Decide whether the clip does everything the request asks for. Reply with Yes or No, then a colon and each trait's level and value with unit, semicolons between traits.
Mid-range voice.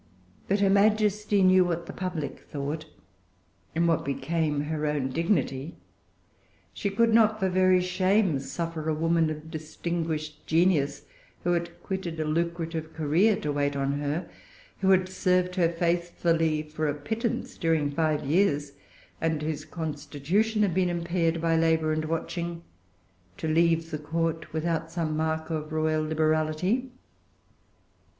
Yes: medium, 165 Hz